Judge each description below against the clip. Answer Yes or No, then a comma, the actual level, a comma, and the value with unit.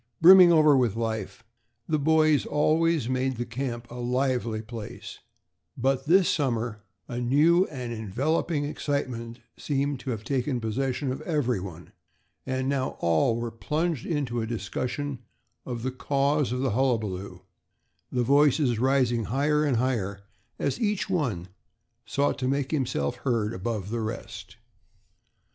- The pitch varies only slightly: No, average, 3.8 semitones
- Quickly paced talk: No, average, 140 wpm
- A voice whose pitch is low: Yes, low, 130 Hz